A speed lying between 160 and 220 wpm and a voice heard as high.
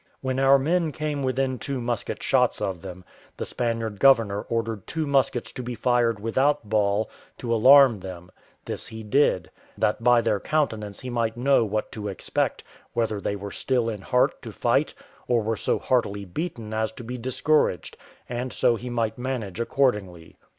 No: average, 175 wpm; low, 115 Hz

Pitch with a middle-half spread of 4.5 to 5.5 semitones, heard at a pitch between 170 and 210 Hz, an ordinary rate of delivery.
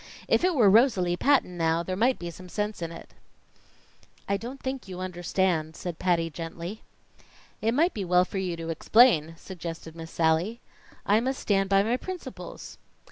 Yes: average, 5.0 semitones; medium, 185 Hz; average, 175 wpm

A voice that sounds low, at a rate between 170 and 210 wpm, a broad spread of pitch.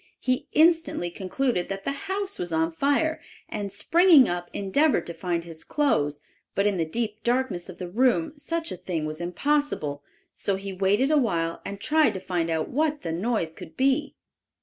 No: high, 200 Hz; average, 185 wpm; wide, 8.7 semitones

